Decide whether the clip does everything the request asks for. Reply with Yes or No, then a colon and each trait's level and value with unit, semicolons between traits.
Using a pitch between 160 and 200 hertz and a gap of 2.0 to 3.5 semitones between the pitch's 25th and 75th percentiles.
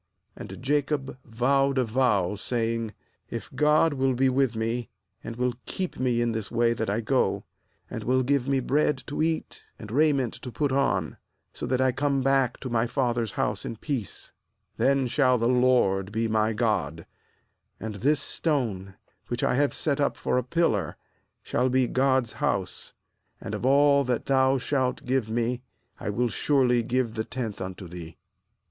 No: low, 125 Hz; average, 3.2 semitones